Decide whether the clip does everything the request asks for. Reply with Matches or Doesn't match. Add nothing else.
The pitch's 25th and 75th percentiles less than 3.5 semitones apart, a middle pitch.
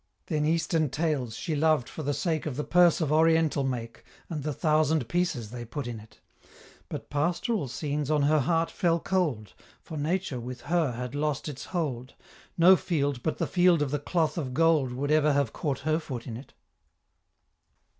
Doesn't match